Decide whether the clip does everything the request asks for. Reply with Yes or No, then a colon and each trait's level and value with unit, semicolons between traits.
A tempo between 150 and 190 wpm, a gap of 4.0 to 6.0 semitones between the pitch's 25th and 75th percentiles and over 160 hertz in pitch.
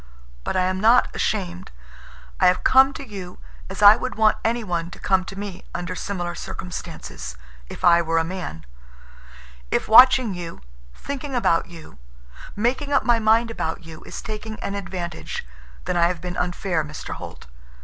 Yes: average, 165 wpm; average, 4.4 semitones; medium, 185 Hz